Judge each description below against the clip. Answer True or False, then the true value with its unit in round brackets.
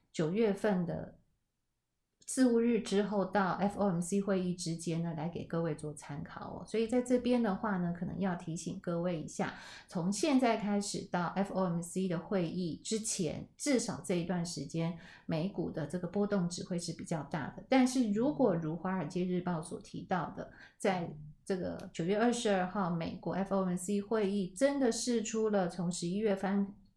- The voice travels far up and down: False (3.5 semitones)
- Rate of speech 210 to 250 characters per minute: False (270 characters per minute)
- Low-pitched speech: False (190 Hz)